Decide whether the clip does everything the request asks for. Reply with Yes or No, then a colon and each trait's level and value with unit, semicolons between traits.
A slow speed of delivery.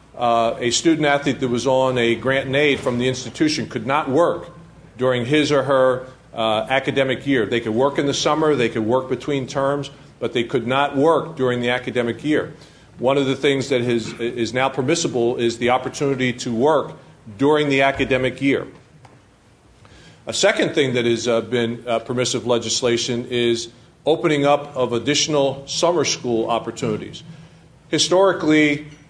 No: average, 165 wpm